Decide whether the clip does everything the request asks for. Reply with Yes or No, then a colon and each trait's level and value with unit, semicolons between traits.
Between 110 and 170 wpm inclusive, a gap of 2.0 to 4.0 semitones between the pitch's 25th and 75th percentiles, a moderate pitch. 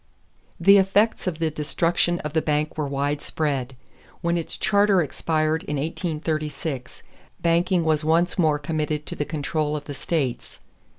Yes: average, 145 wpm; narrow, 2.4 semitones; medium, 155 Hz